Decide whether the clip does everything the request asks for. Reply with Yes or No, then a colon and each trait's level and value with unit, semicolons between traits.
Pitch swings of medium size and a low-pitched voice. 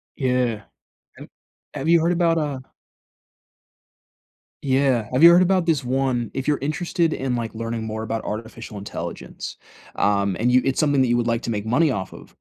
Yes: average, 4.7 semitones; low, 130 Hz